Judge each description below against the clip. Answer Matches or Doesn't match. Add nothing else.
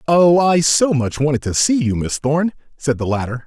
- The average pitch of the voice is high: Doesn't match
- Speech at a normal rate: Doesn't match